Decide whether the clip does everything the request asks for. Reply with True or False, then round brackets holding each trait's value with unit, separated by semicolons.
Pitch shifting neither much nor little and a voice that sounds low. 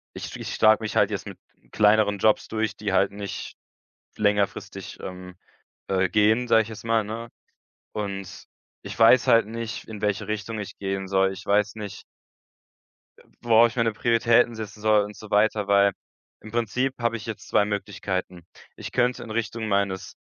False (2.0 semitones; 105 Hz)